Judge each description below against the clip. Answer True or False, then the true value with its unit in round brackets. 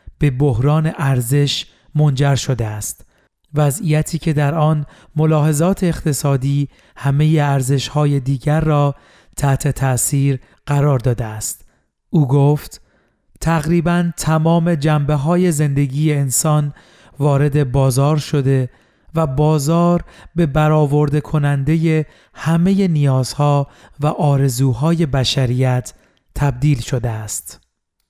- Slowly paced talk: True (100 wpm)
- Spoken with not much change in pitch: True (2.3 semitones)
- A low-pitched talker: False (145 Hz)